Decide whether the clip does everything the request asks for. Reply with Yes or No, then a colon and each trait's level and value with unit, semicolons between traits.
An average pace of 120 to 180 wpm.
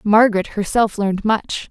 Yes: average, 140 wpm